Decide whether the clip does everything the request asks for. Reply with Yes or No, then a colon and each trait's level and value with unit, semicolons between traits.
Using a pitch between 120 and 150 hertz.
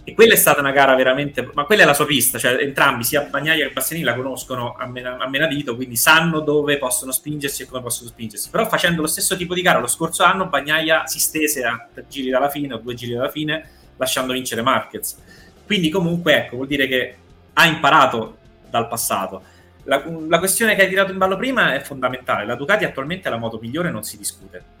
Yes: medium, 140 Hz